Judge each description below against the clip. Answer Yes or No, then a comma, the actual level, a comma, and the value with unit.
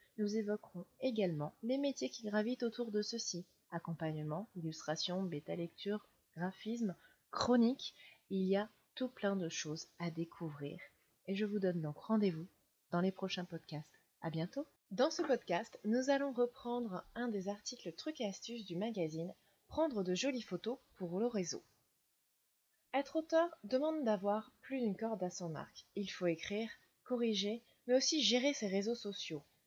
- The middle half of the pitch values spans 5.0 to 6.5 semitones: Yes, wide, 5.6 semitones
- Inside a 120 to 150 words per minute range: No, average, 160 wpm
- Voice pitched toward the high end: Yes, high, 205 Hz